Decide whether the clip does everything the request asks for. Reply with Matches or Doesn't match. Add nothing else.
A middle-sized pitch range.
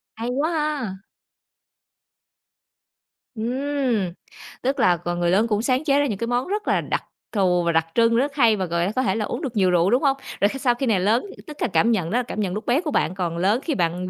Doesn't match